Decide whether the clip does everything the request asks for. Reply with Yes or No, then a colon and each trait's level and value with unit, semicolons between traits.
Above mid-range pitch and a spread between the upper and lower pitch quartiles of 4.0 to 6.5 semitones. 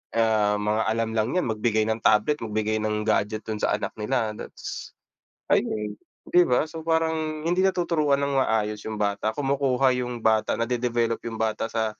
No: low, 115 Hz; average, 4.3 semitones